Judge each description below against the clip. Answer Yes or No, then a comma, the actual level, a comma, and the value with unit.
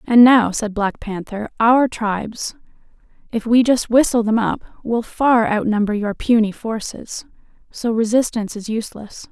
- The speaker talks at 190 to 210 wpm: No, average, 150 wpm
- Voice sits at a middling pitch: No, high, 225 Hz